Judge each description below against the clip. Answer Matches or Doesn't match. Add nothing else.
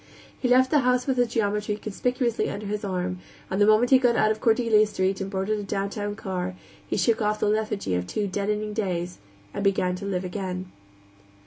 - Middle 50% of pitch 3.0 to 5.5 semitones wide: Doesn't match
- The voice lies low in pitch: Doesn't match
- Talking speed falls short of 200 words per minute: Doesn't match